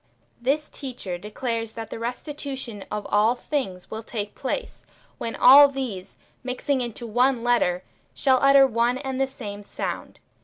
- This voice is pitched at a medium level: No, high, 245 Hz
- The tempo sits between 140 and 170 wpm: Yes, average, 150 wpm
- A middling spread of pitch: Yes, average, 3.6 semitones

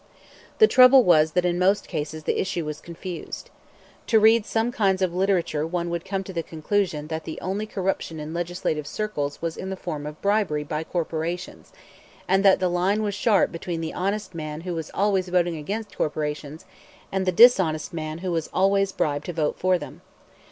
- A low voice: No, medium, 175 Hz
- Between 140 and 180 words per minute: No, average, 195 wpm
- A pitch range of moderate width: Yes, average, 3.5 semitones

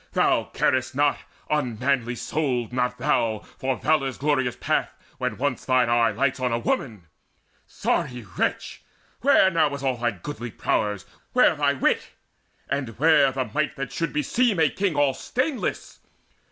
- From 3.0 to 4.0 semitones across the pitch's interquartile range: Yes, average, 3.5 semitones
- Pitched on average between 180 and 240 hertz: No, low, 135 Hz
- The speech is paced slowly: No, average, 155 wpm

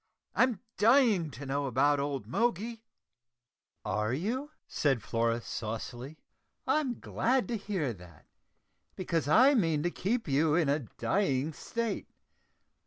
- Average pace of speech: No, slow, 125 wpm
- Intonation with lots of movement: Yes, wide, 8.9 semitones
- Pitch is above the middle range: No, medium, 160 Hz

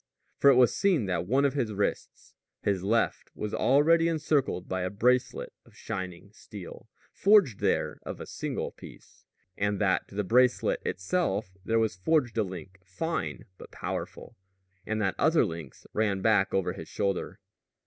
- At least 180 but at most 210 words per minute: No, average, 165 wpm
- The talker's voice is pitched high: No, low, 105 Hz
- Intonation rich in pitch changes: Yes, wide, 5.7 semitones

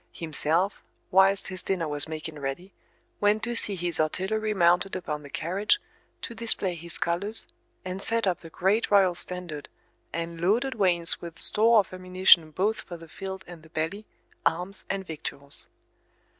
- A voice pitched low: No, medium, 180 Hz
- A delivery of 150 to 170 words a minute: Yes, average, 160 wpm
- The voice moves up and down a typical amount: Yes, average, 3.3 semitones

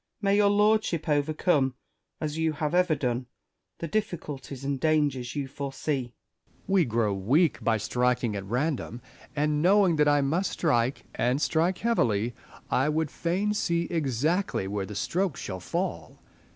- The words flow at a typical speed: Yes, average, 150 wpm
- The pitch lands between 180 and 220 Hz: No, medium, 150 Hz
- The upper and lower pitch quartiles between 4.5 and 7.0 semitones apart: Yes, wide, 5.5 semitones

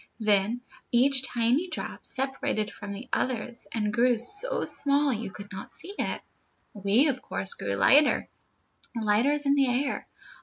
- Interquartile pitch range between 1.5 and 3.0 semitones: No, average, 4.8 semitones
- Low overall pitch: No, high, 245 Hz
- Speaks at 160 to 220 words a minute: No, average, 150 wpm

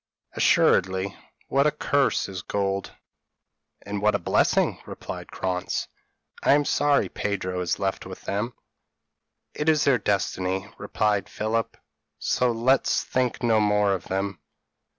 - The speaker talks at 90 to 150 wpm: Yes, slow, 135 wpm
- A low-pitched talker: Yes, low, 105 Hz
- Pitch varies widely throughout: No, average, 4.4 semitones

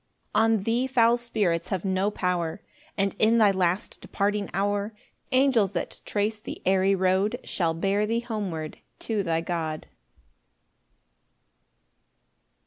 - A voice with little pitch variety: No, average, 3.2 semitones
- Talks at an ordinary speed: No, slow, 130 wpm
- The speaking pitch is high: Yes, high, 200 Hz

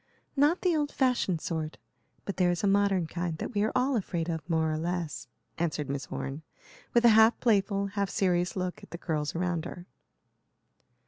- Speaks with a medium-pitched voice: Yes, medium, 180 Hz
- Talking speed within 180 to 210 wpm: Yes, average, 190 wpm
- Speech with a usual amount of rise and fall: Yes, average, 4.2 semitones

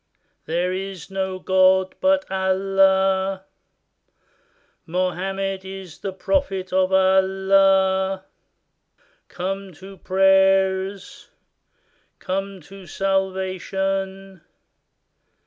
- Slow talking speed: Yes, slow, 70 wpm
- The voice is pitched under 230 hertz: Yes, high, 190 Hz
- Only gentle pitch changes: Yes, narrow, 0.5 semitones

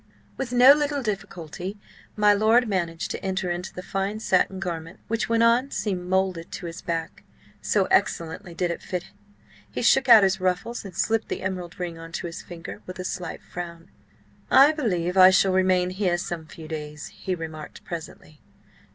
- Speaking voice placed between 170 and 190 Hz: Yes, medium, 185 Hz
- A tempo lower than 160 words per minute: No, average, 180 wpm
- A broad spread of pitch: No, average, 3.5 semitones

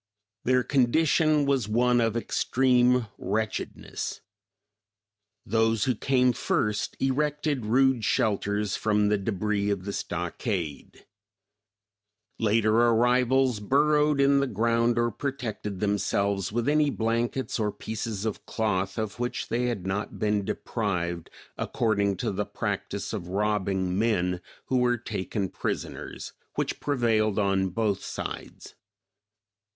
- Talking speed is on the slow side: Yes, slow, 120 wpm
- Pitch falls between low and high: No, low, 110 Hz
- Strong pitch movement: No, average, 3.5 semitones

